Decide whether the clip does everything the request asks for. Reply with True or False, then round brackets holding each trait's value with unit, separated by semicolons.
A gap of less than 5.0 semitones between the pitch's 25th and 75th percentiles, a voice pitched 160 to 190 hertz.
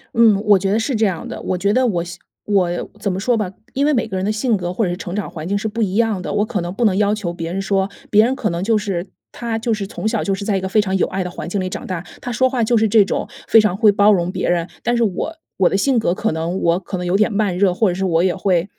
False (3.2 semitones; 200 Hz)